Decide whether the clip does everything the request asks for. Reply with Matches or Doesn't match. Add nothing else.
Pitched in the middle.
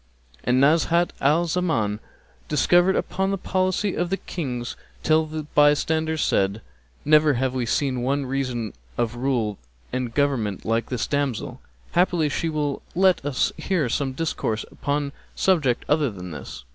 Matches